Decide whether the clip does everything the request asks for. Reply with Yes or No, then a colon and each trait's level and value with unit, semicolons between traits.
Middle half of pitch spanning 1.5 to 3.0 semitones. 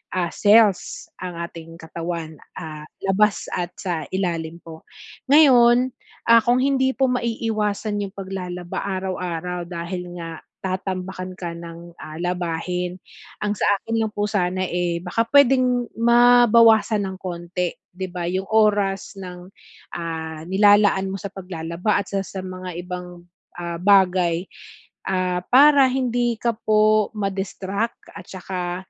No: average, 3.4 semitones